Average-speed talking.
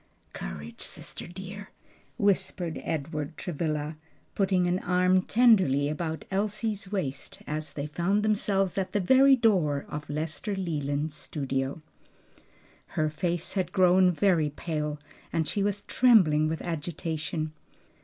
No: slow, 125 wpm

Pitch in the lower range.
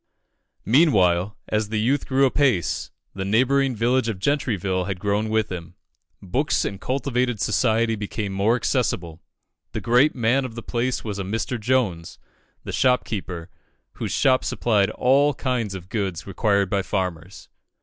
Yes: low, 110 Hz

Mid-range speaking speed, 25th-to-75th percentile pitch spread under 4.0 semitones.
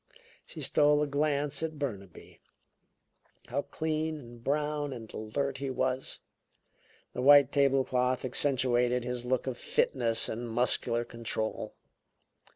No: slow, 125 wpm; average, 3.0 semitones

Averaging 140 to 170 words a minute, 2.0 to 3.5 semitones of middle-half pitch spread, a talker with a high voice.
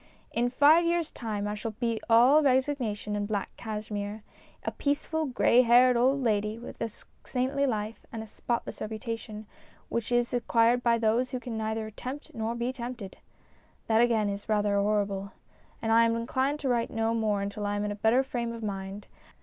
No: average, 190 wpm; average, 2.9 semitones; high, 230 Hz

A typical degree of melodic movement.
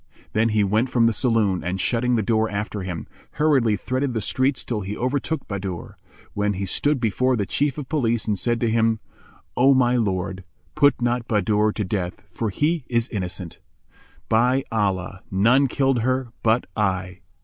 Yes: average, 4.2 semitones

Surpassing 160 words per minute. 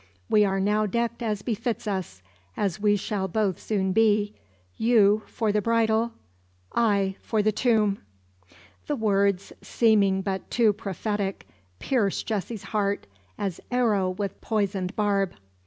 No: slow, 135 wpm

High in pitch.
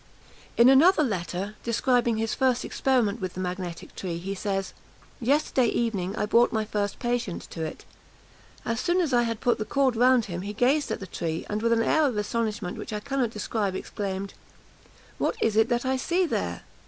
Yes: high, 225 Hz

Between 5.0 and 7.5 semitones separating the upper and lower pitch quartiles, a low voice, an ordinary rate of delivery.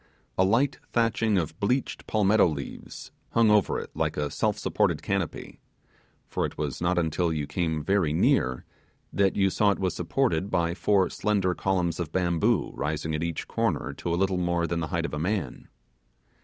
No: average, 3.5 semitones; very low, 90 Hz; average, 185 wpm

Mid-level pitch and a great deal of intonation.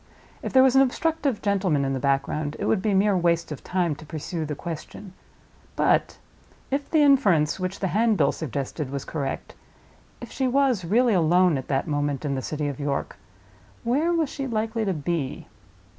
Yes: medium, 180 Hz; wide, 7.9 semitones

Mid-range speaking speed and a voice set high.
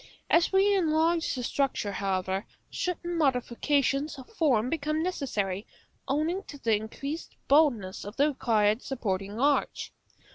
No: slow, 130 wpm; very high, 275 Hz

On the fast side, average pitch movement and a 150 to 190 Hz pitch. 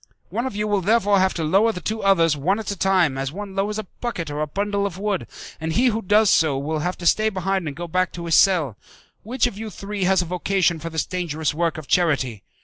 Yes: fast, 255 wpm; average, 4.2 semitones; medium, 185 Hz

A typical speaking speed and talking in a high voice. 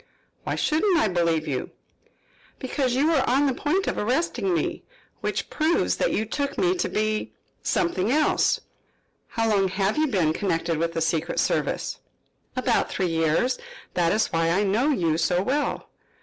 Yes: average, 165 wpm; high, 215 Hz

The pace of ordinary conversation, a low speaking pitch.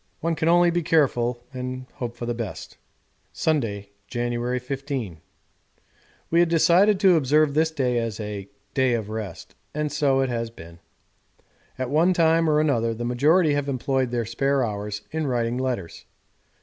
Yes: average, 160 wpm; low, 130 Hz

